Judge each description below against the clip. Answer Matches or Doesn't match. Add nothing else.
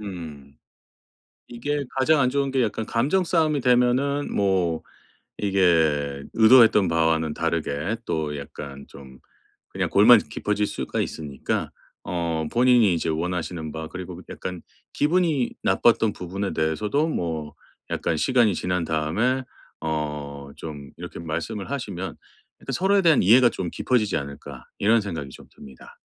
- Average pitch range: Doesn't match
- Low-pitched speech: Matches